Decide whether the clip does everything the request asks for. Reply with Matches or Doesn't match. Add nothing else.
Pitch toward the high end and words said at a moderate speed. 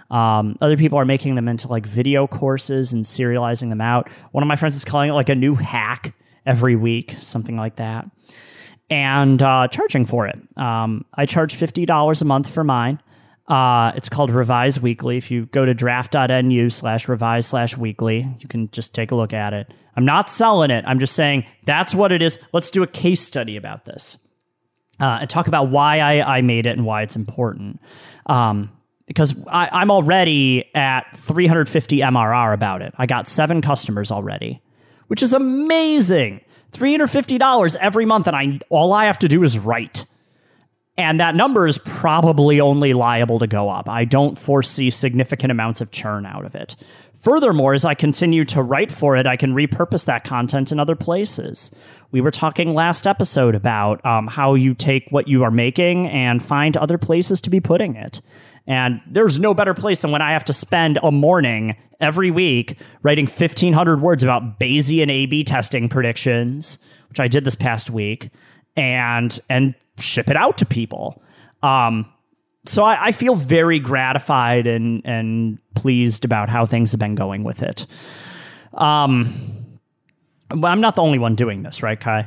Doesn't match